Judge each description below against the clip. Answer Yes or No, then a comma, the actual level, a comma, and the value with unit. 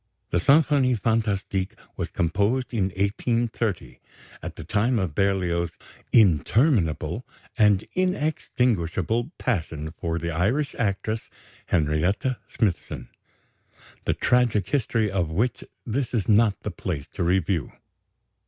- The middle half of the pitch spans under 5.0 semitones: No, wide, 5.6 semitones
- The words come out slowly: Yes, slow, 110 wpm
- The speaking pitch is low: Yes, low, 100 Hz